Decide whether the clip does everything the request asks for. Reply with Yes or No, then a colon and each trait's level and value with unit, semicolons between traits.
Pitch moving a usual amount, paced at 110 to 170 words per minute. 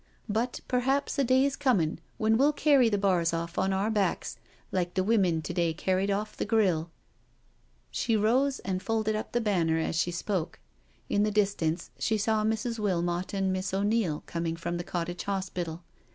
No: average, 4.2 semitones; average, 180 wpm